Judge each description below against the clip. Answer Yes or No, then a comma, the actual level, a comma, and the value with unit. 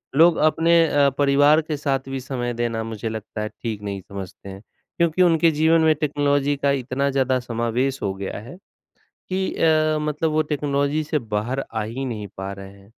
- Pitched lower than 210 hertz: Yes, low, 135 Hz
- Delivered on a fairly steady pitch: No, wide, 5.4 semitones